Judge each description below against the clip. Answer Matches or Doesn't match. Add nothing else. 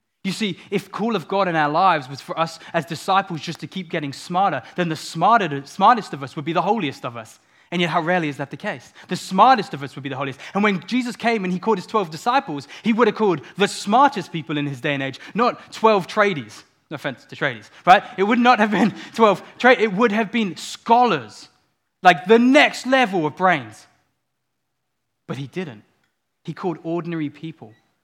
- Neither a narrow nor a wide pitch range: Doesn't match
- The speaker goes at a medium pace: Doesn't match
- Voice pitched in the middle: Matches